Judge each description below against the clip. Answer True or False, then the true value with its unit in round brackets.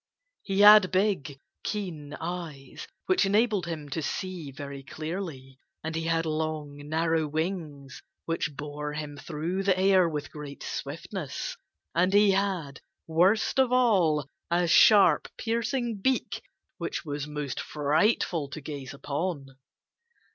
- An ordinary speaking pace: False (130 wpm)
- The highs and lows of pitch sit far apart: False (4.7 semitones)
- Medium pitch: True (160 Hz)